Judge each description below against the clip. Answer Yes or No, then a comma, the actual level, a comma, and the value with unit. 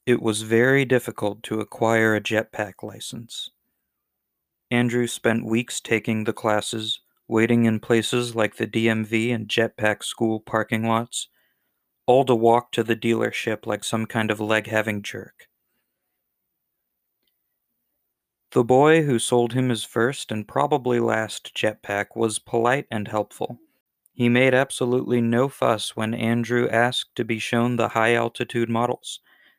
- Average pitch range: No, narrow, 1.7 semitones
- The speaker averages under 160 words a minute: Yes, average, 140 wpm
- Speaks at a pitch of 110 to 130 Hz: Yes, low, 115 Hz